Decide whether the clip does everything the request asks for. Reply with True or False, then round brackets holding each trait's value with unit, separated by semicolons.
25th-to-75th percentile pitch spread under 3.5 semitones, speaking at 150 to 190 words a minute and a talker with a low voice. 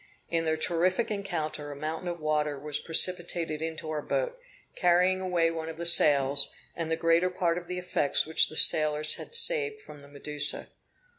False (2.9 semitones; 180 wpm; 165 Hz)